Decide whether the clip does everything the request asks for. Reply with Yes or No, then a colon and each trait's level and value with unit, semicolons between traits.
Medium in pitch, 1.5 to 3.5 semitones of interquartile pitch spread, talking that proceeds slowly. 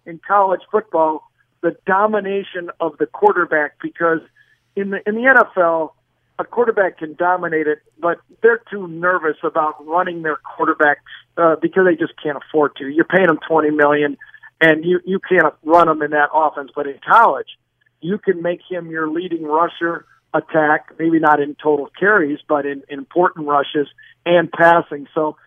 No: medium, 160 Hz; average, 3.0 semitones; average, 170 wpm